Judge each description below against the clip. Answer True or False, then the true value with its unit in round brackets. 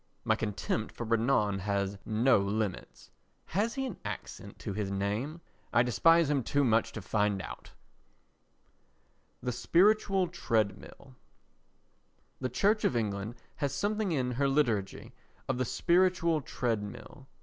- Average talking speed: False (130 wpm)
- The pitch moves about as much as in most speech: False (7.9 semitones)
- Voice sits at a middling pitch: False (125 Hz)